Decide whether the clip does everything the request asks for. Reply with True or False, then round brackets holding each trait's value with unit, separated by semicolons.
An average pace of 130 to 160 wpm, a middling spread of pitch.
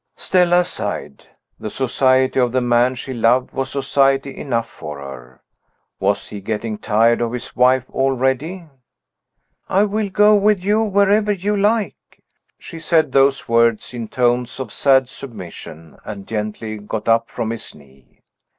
False (150 wpm; 6.4 semitones)